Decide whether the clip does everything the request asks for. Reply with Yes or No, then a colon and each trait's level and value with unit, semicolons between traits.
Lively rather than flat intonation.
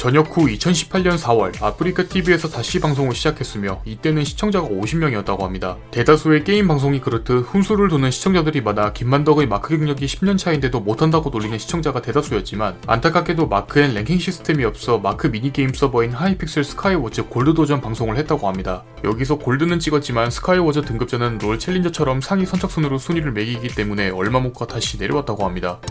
Yes: wide, 6.2 semitones